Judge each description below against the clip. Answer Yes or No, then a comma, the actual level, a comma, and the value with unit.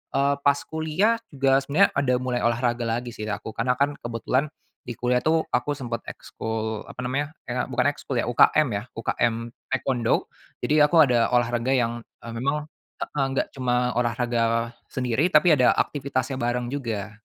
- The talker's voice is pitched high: No, low, 125 Hz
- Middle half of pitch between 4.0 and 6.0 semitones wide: No, average, 3.1 semitones